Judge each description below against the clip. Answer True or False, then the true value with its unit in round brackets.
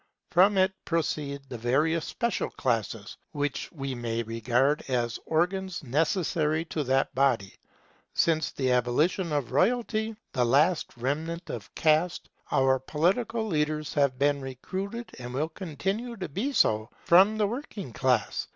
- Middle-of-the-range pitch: True (150 Hz)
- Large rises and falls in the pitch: True (6.1 semitones)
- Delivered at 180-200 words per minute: False (140 wpm)